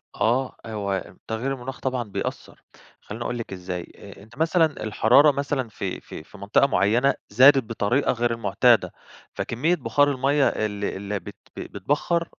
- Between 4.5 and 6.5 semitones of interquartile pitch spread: Yes, average, 5.0 semitones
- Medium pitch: No, low, 120 Hz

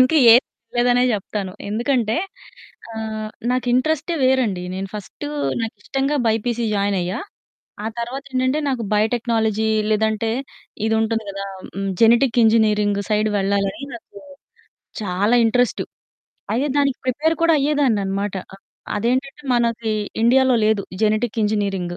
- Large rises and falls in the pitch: No, average, 3.3 semitones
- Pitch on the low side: No, high, 225 Hz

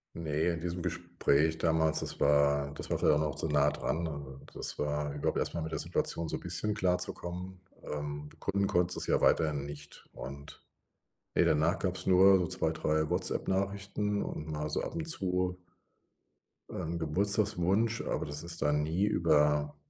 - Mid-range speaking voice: No, very low, 80 Hz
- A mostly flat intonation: No, average, 3.7 semitones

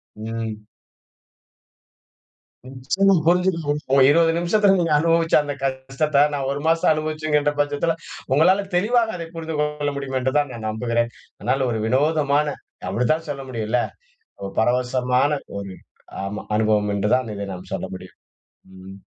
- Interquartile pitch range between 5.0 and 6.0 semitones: Yes, wide, 5.4 semitones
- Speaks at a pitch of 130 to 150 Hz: Yes, medium, 140 Hz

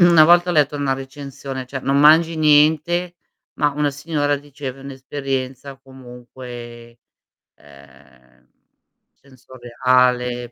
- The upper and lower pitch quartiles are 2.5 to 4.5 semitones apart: Yes, average, 2.9 semitones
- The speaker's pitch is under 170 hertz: Yes, low, 135 Hz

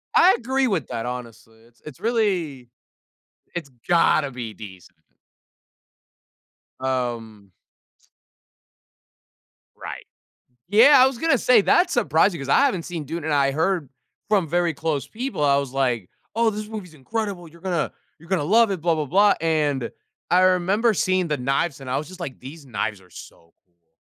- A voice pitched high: No, medium, 160 Hz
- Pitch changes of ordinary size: No, wide, 7.0 semitones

